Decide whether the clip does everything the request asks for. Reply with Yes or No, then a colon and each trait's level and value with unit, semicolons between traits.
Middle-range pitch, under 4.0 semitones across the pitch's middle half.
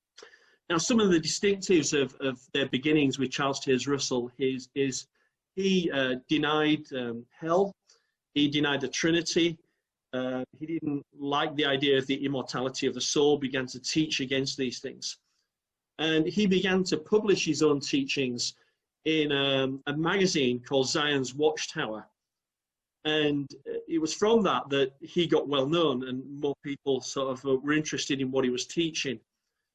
Yes: medium, 145 Hz; average, 3.5 semitones